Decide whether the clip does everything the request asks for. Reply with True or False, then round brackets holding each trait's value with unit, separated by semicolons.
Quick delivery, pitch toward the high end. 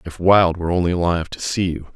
False (245 wpm; 85 Hz)